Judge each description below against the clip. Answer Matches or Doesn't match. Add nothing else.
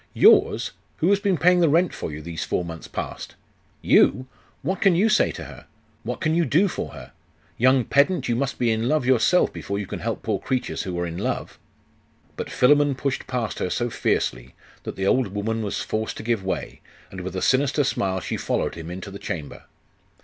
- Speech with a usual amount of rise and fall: Doesn't match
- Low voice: Matches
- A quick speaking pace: Matches